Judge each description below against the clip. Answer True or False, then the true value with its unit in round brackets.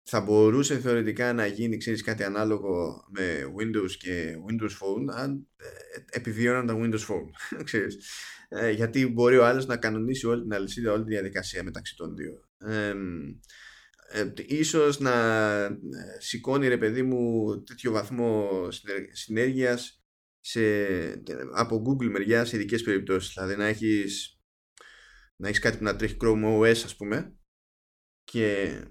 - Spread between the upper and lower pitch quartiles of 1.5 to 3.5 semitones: True (2.9 semitones)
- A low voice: True (110 Hz)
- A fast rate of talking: False (135 wpm)